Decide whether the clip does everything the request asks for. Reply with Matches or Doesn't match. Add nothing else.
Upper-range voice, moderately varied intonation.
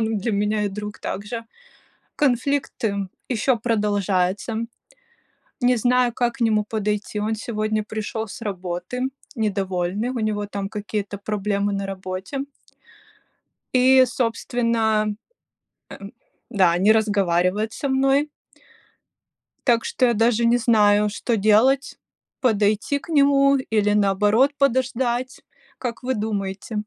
Matches